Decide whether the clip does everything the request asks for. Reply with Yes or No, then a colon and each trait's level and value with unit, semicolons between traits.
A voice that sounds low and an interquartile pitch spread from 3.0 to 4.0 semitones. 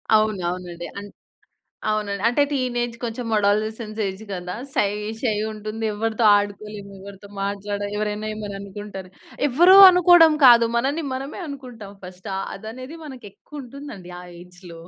No: high, 215 Hz; average, 3.7 semitones